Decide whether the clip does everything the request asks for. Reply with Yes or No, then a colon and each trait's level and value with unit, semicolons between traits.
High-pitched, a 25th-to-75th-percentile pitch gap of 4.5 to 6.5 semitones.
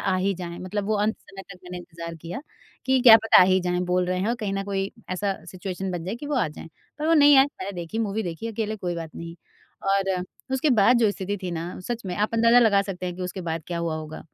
No: high, 195 Hz; average, 3.6 semitones